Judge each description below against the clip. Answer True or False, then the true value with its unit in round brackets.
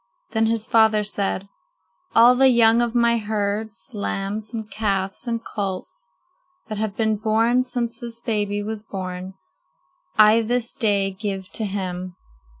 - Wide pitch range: False (2.4 semitones)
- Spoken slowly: False (145 wpm)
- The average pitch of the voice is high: True (215 Hz)